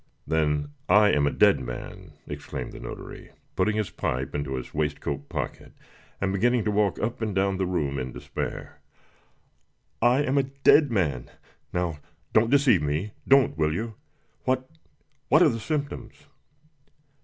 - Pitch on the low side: Yes, low, 100 Hz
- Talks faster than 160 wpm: No, average, 155 wpm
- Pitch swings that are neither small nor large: No, wide, 8.5 semitones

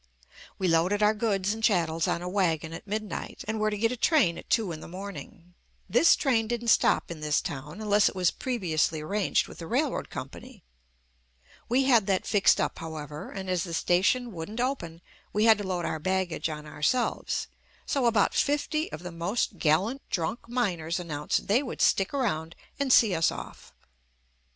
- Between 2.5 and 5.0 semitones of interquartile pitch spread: No, wide, 5.4 semitones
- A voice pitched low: No, high, 195 Hz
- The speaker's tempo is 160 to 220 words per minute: Yes, average, 185 wpm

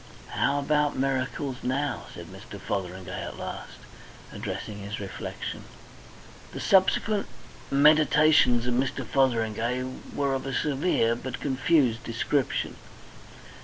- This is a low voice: Yes, low, 130 Hz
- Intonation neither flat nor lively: Yes, average, 3.6 semitones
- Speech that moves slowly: Yes, slow, 110 wpm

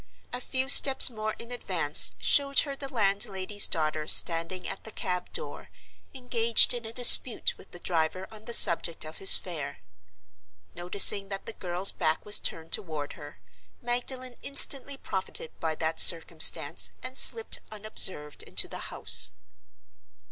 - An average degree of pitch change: No, wide, 6.6 semitones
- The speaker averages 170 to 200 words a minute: No, average, 150 wpm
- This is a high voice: Yes, high, 195 Hz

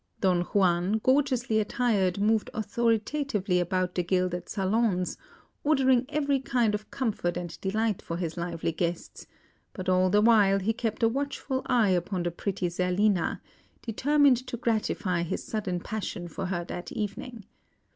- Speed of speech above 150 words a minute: No, average, 145 wpm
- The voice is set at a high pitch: Yes, high, 205 Hz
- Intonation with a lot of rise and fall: No, average, 4.5 semitones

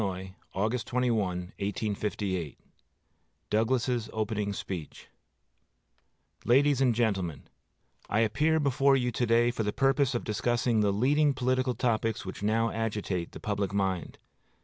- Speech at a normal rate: No, slow, 125 wpm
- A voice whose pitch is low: Yes, low, 115 Hz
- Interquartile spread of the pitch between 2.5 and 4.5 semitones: Yes, average, 3.6 semitones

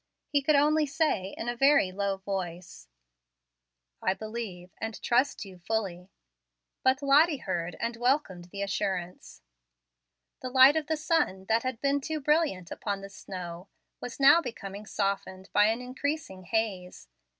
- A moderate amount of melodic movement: No, wide, 6.7 semitones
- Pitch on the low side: No, high, 220 Hz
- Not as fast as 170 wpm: Yes, average, 150 wpm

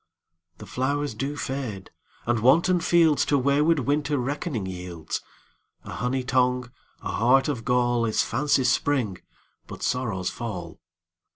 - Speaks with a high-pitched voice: No, low, 125 Hz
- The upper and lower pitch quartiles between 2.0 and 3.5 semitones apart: No, average, 3.9 semitones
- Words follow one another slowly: Yes, slow, 115 wpm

